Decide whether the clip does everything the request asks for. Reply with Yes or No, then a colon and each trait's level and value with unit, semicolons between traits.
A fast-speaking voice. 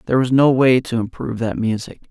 Yes: fast, 230 wpm